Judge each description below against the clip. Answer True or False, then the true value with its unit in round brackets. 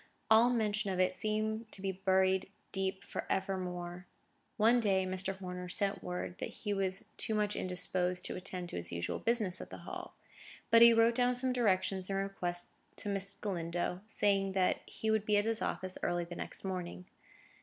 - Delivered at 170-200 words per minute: True (180 wpm)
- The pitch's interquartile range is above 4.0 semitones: False (2.8 semitones)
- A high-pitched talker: True (195 Hz)